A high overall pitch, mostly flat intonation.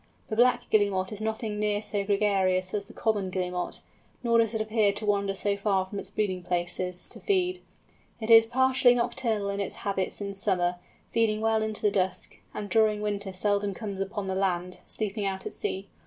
Yes: high, 205 Hz; narrow, 2.3 semitones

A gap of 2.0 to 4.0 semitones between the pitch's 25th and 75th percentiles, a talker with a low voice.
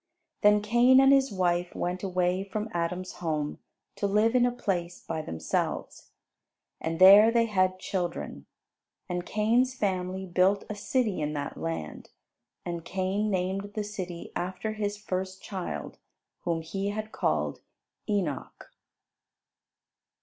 No: average, 3.0 semitones; high, 190 Hz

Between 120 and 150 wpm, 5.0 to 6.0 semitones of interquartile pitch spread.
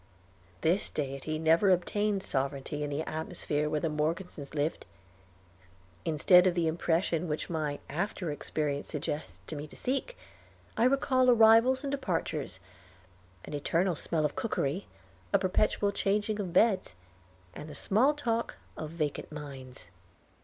Yes: average, 140 wpm; wide, 5.4 semitones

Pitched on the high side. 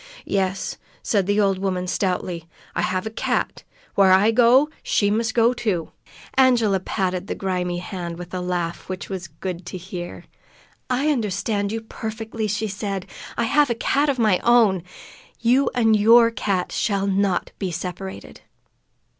Yes: high, 200 Hz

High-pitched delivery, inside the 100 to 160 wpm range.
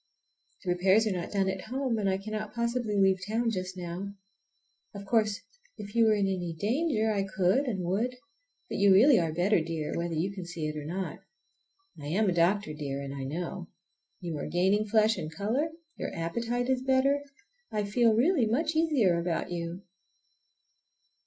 No: high, 200 Hz; average, 185 wpm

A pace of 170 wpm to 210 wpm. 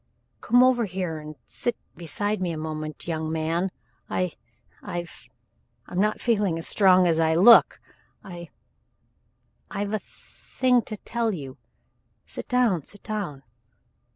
No: slow, 135 wpm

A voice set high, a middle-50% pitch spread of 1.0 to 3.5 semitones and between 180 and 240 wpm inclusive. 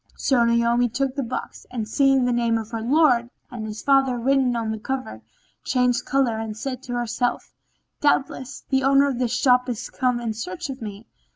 Yes: high, 245 Hz; narrow, 2.5 semitones; average, 195 wpm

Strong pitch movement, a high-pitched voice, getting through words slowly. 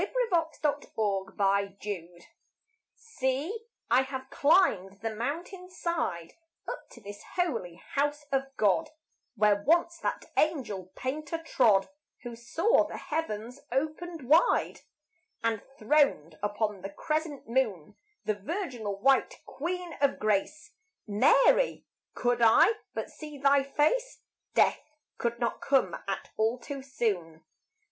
Yes: wide, 7.0 semitones; very high, 260 Hz; slow, 120 wpm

